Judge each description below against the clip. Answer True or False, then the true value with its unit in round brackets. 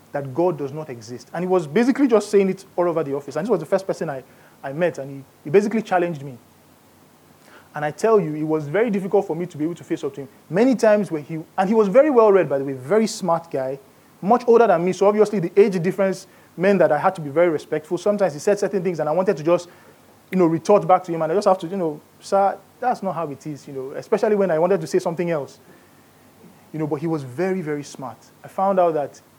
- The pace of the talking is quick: True (270 wpm)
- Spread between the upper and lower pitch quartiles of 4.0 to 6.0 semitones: True (4.6 semitones)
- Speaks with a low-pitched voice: False (175 Hz)